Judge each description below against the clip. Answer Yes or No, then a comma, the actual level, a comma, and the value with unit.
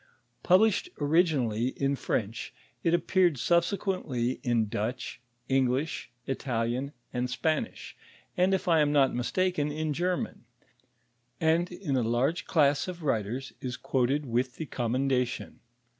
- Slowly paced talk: Yes, slow, 125 wpm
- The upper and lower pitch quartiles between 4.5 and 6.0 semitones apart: Yes, wide, 5.4 semitones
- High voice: No, medium, 140 Hz